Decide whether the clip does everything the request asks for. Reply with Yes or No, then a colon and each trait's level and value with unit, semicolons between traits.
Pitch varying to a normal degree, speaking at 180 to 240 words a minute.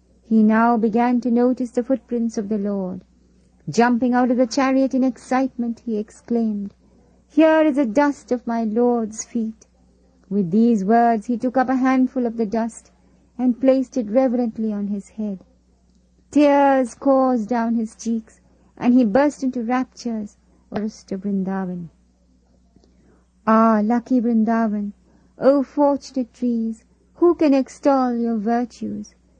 No: average, 3.2 semitones; average, 140 wpm